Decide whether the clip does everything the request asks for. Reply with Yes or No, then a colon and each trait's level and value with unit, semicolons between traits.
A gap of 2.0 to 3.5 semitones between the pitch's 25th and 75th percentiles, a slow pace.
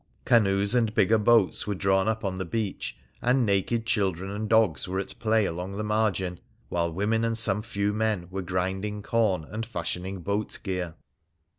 No: average, 2.9 semitones; average, 175 wpm